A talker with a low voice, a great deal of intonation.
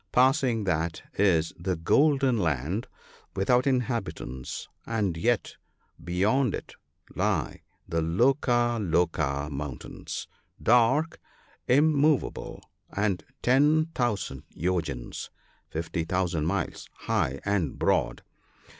Yes: low, 100 Hz; wide, 7.3 semitones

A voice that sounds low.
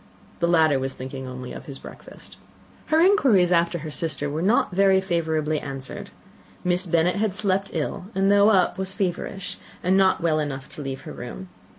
No: medium, 170 Hz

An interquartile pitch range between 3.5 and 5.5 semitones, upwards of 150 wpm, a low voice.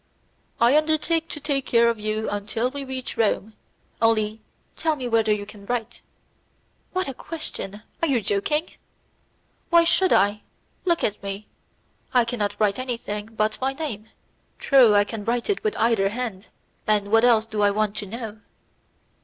No: average, 4.1 semitones; average, 165 wpm; high, 225 Hz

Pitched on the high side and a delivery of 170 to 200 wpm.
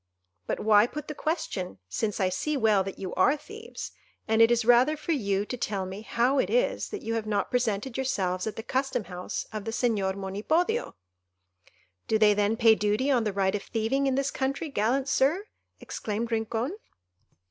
Yes: high, 225 Hz; average, 190 wpm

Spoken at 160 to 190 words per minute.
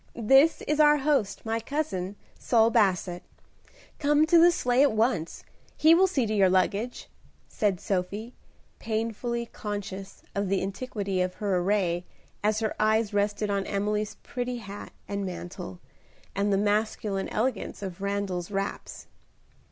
No: average, 145 wpm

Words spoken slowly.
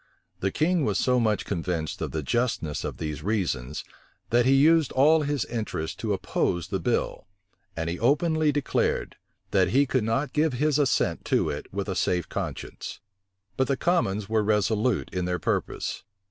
No: average, 175 wpm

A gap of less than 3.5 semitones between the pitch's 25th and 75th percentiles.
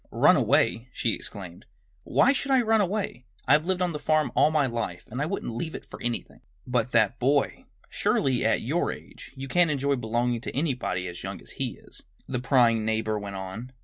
No: wide, 5.5 semitones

